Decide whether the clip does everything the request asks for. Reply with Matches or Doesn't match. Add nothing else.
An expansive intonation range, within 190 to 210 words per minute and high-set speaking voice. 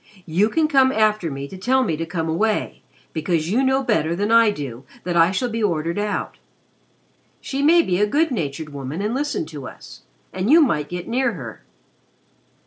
Matches